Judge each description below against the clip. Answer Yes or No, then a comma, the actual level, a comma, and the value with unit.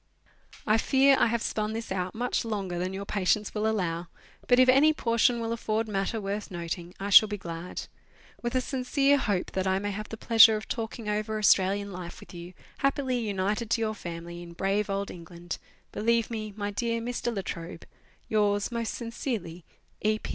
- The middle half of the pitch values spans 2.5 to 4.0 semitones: Yes, average, 3.4 semitones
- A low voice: No, high, 210 Hz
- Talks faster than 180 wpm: Yes, average, 190 wpm